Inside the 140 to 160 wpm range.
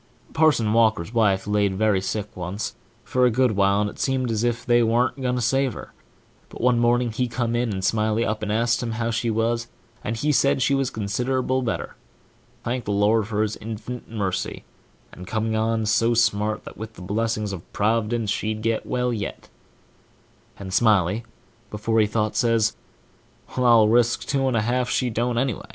No: average, 185 wpm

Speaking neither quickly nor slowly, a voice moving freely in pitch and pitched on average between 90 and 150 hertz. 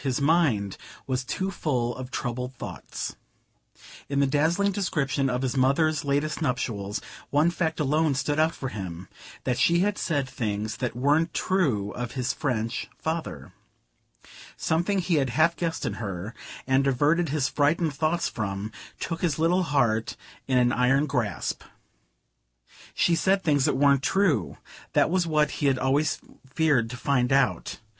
No: average, 155 wpm; average, 4.3 semitones; medium, 140 Hz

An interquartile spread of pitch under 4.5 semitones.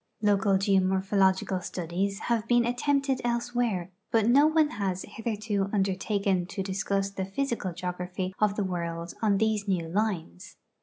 Yes: average, 2.9 semitones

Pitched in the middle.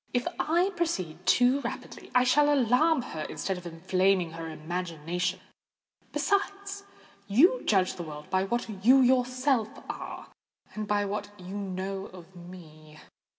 No: high, 195 Hz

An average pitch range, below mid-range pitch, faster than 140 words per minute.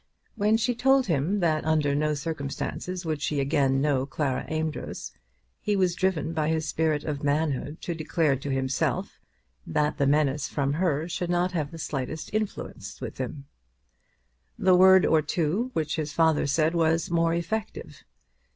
No: average, 3.3 semitones; medium, 155 Hz; average, 160 wpm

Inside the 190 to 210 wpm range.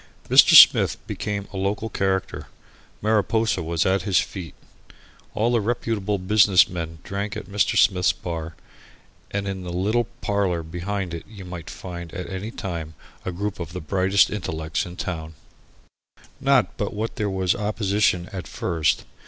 No: average, 160 wpm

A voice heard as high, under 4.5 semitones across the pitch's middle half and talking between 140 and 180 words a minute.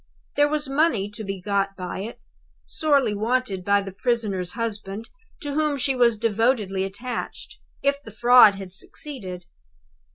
No: high, 220 Hz; average, 4.8 semitones; average, 150 wpm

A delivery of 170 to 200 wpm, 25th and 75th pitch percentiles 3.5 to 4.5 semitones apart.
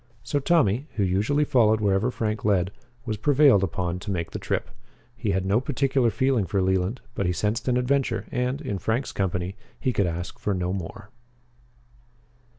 No: average, 175 wpm; average, 5.1 semitones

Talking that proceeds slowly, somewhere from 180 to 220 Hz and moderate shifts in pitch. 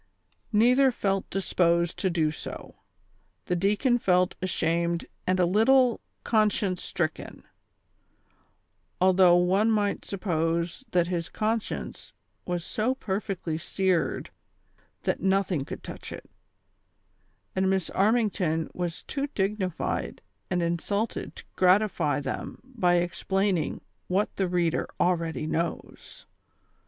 Yes: slow, 115 wpm; medium, 185 Hz; average, 3.3 semitones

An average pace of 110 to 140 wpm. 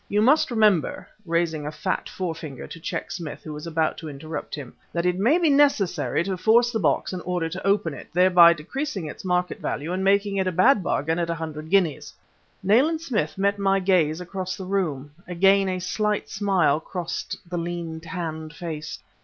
No: average, 195 wpm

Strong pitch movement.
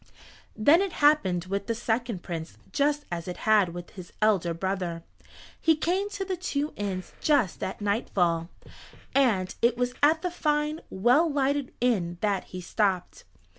Yes: wide, 8.1 semitones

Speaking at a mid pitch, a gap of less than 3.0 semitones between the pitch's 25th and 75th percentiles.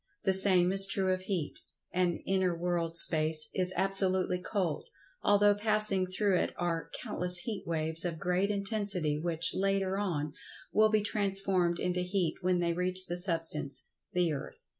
Yes: medium, 180 Hz; narrow, 2.4 semitones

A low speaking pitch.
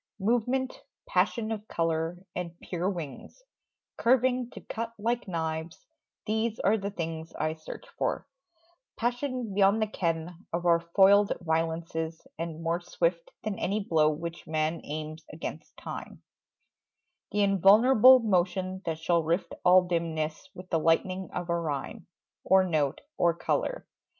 No: medium, 175 Hz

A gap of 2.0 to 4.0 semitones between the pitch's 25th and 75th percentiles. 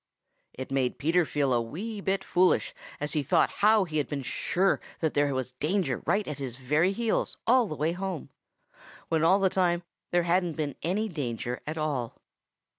No: average, 5.1 semitones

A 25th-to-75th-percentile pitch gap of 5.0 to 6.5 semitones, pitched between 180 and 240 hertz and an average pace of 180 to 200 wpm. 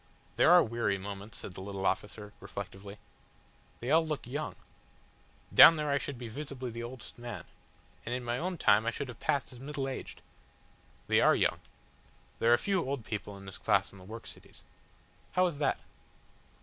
No: wide, 5.4 semitones; low, 120 Hz; average, 190 wpm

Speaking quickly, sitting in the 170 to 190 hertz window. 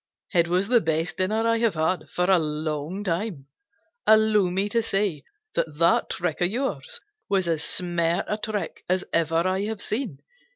No: average, 175 wpm; medium, 185 Hz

